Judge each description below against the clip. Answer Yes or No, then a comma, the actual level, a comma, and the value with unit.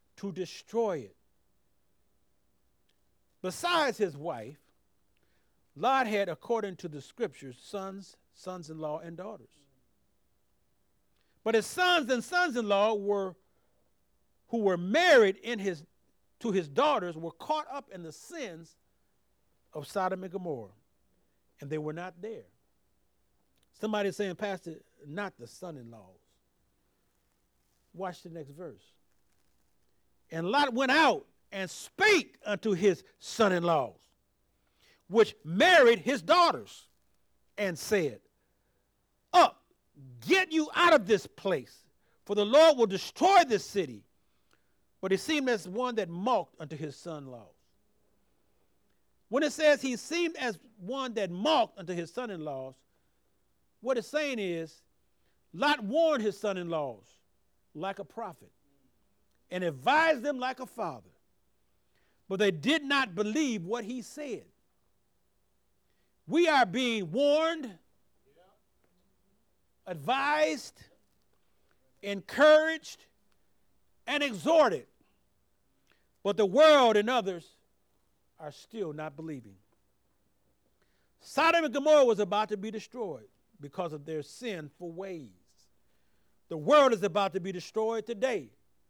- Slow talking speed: Yes, slow, 120 wpm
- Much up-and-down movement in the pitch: Yes, wide, 8.6 semitones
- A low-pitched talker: No, high, 195 Hz